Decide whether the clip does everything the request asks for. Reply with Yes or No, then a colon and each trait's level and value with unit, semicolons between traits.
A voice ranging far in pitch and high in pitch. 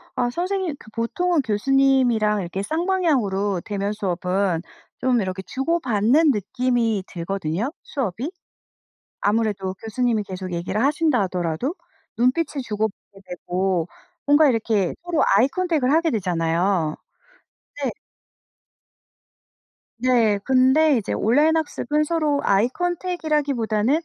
Yes: wide, 6.9 semitones; high, 230 Hz